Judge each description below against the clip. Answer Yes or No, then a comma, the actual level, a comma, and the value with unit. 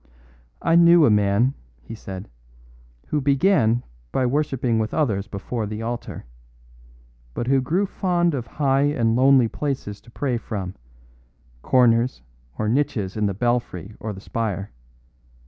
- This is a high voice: No, low, 120 Hz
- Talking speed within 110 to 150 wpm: Yes, average, 140 wpm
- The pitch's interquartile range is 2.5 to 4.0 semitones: No, average, 4.6 semitones